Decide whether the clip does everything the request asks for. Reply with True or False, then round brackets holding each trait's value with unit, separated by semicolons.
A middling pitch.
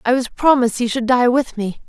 False (245 Hz)